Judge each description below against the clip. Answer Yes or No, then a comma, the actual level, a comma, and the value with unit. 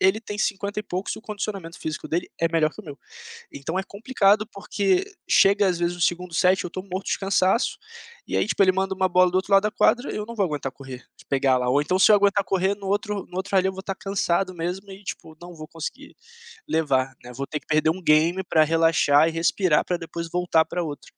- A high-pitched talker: No, medium, 180 Hz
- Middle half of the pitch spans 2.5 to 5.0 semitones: Yes, average, 3.4 semitones